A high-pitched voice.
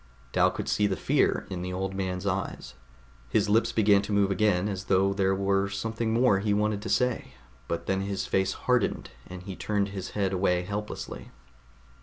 No: low, 100 Hz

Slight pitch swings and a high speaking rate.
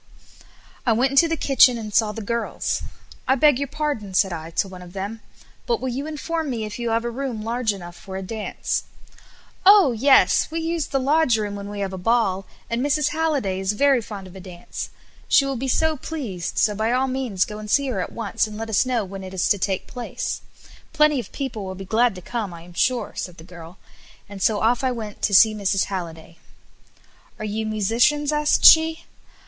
No: wide, 5.6 semitones; fast, 220 wpm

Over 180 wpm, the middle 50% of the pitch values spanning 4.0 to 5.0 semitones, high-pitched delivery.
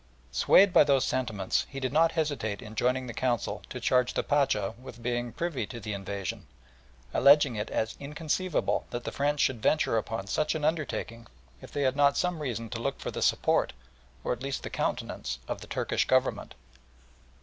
No: average, 190 wpm; average, 4.4 semitones; low, 130 Hz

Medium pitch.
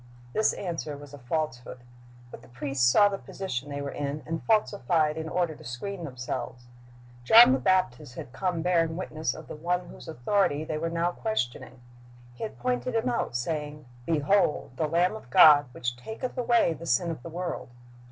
Yes: medium, 160 Hz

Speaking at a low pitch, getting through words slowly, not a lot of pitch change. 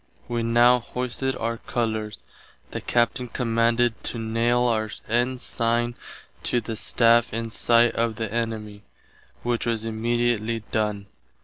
Yes: low, 115 Hz; slow, 125 wpm; narrow, 1.2 semitones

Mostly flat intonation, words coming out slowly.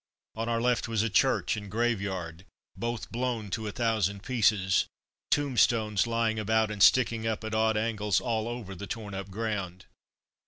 No: narrow, 2.3 semitones; average, 165 wpm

